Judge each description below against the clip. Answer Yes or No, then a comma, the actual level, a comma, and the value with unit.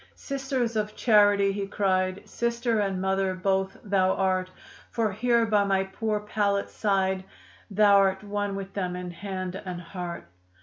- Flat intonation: Yes, narrow, 1.8 semitones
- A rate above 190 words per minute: No, average, 145 wpm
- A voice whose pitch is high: Yes, high, 195 Hz